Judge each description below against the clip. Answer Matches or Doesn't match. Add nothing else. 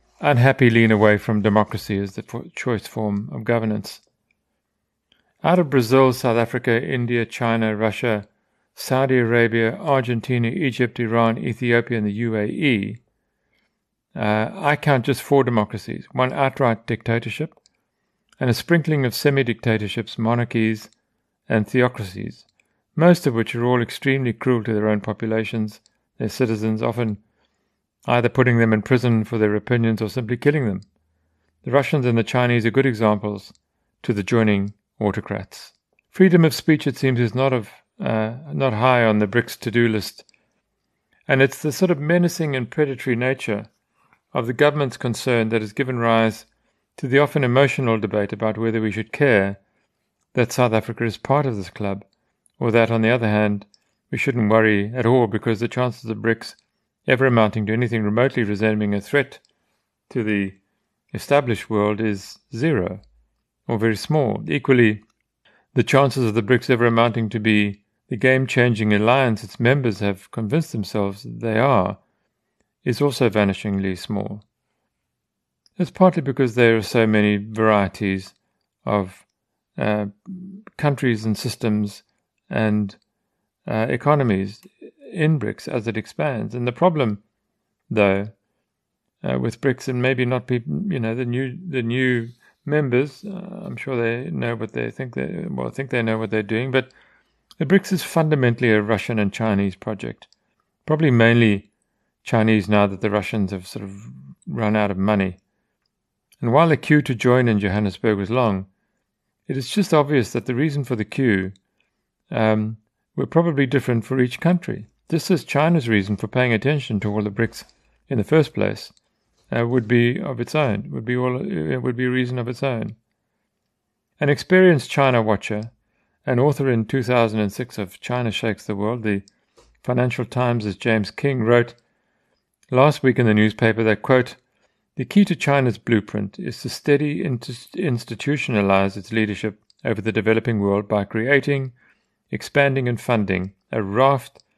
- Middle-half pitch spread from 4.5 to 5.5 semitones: Doesn't match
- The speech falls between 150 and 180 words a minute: Matches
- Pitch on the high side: Doesn't match